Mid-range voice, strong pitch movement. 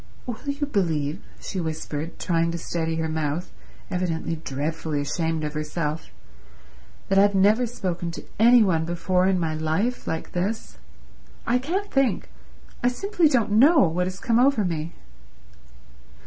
Yes: medium, 180 Hz; wide, 6.1 semitones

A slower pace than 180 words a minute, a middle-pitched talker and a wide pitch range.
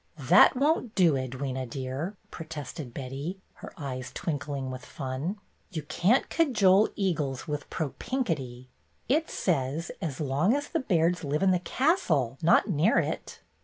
Yes: average, 150 wpm; medium, 160 Hz; wide, 6.4 semitones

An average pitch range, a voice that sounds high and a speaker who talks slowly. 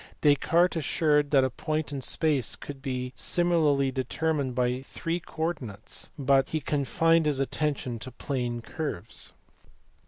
No: average, 3.3 semitones; medium, 140 Hz; slow, 130 wpm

